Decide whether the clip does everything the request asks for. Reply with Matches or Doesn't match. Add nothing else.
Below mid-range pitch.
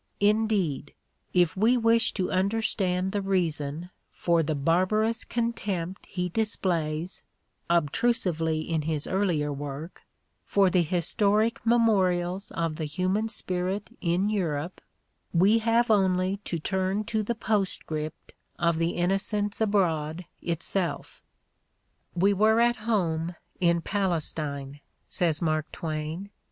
Doesn't match